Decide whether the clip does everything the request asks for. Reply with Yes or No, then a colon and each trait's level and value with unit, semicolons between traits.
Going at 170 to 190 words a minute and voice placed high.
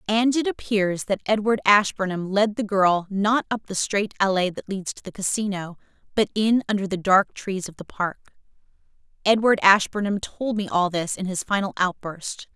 Yes: average, 180 wpm; high, 200 Hz